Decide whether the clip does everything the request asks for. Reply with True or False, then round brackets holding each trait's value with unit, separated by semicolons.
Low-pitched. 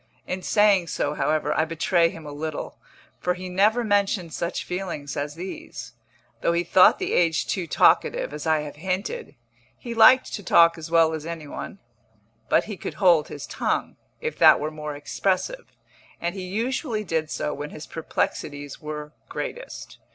False (170 Hz)